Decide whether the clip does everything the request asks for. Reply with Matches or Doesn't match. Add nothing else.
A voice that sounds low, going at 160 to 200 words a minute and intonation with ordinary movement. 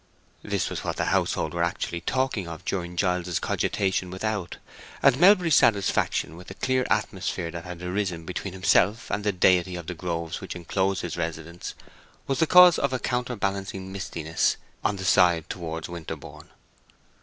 Matches